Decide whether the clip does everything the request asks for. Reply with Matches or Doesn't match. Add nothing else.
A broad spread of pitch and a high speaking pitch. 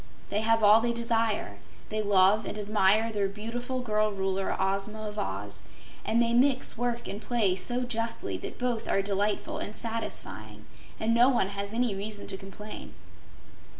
Doesn't match